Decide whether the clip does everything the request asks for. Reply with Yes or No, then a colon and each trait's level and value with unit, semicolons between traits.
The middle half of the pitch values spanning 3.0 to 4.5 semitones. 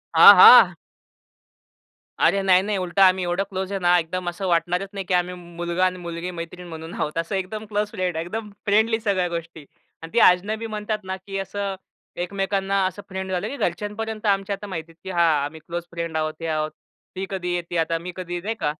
No: narrow, 2.5 semitones